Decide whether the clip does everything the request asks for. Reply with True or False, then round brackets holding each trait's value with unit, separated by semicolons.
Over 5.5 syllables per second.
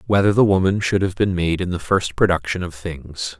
False (5.3 syllables/s)